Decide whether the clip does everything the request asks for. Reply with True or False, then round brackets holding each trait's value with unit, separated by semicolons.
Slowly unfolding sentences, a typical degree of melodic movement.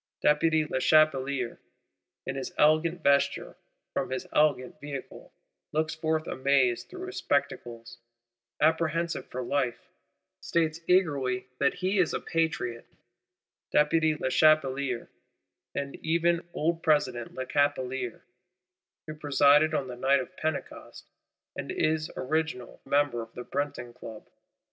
True (110 wpm; 3.4 semitones)